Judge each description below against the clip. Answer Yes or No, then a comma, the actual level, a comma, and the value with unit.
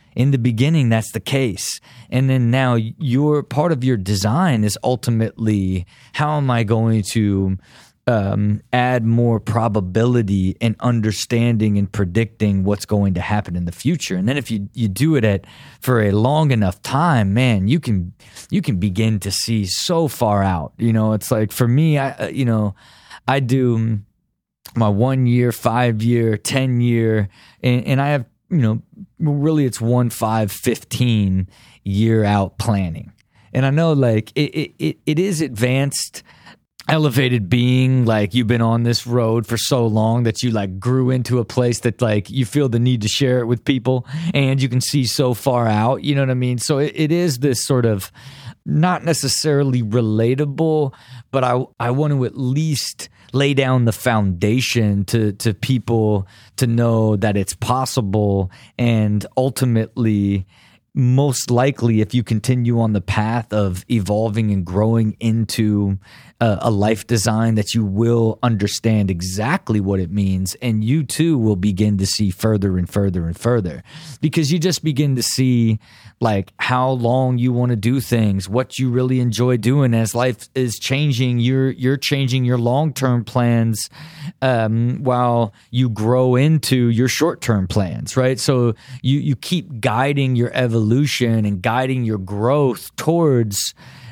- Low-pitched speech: Yes, low, 120 Hz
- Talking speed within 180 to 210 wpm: No, average, 165 wpm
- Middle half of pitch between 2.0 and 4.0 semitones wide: Yes, average, 3.3 semitones